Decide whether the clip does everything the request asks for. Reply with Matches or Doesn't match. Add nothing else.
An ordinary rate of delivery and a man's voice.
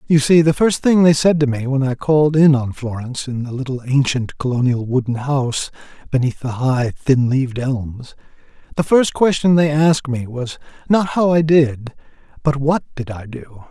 Matches